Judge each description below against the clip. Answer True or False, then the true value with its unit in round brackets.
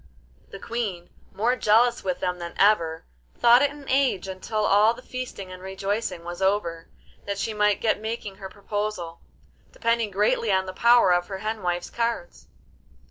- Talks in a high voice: True (205 Hz)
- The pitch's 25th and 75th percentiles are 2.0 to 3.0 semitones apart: False (3.7 semitones)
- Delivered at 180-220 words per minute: False (170 wpm)